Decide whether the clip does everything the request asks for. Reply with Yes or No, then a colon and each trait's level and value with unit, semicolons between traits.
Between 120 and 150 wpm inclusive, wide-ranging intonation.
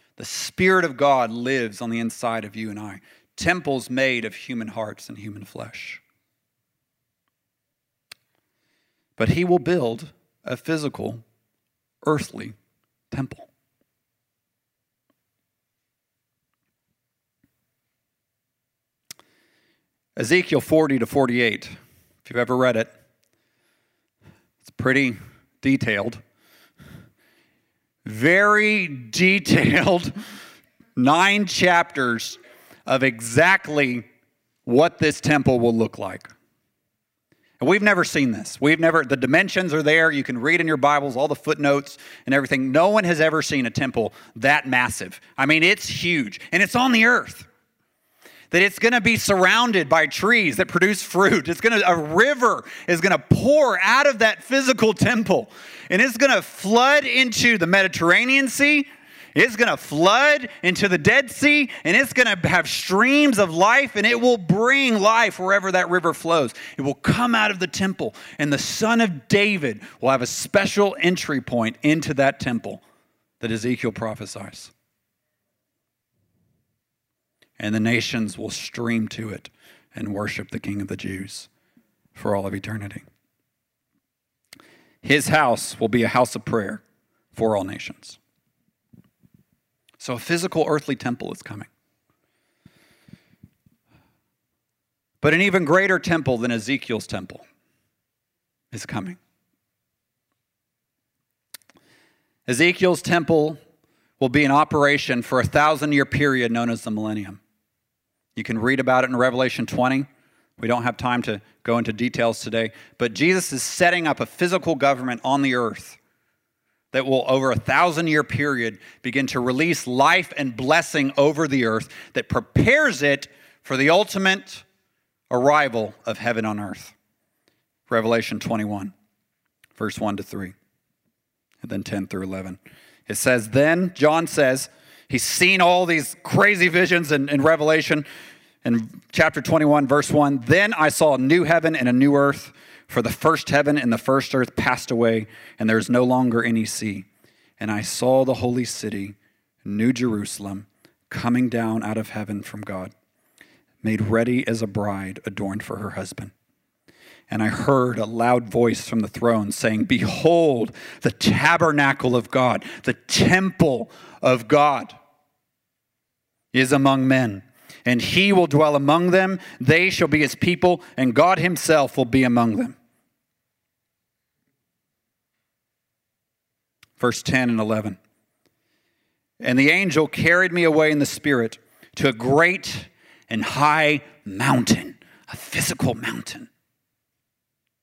Yes: average, 140 wpm; wide, 6.6 semitones